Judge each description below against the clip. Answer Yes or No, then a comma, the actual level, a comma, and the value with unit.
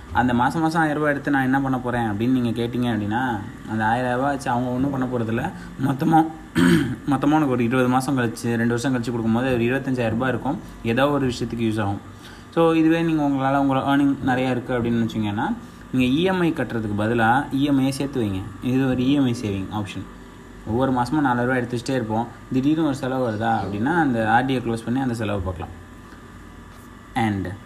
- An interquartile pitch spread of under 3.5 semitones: Yes, average, 2.9 semitones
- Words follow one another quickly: Yes, fast, 175 wpm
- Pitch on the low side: Yes, low, 125 Hz